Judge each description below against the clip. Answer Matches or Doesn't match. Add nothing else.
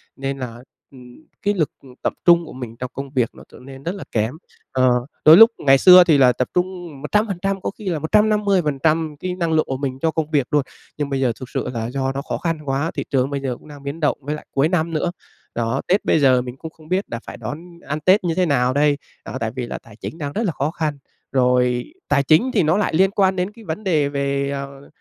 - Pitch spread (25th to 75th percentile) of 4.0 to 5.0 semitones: Matches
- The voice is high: Doesn't match